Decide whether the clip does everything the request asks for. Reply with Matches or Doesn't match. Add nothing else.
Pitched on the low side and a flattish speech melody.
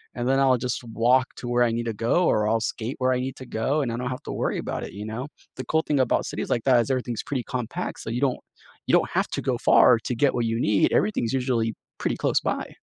Matches